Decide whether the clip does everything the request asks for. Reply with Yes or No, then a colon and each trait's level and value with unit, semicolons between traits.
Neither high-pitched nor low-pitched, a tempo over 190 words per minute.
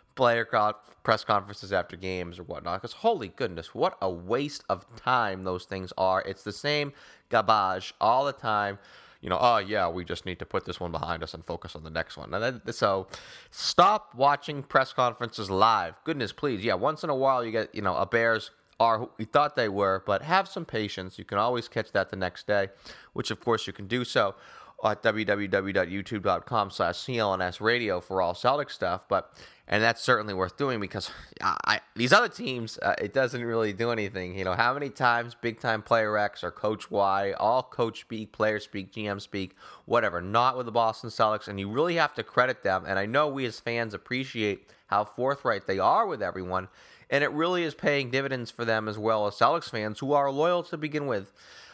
No: low, 110 Hz; fast, 205 wpm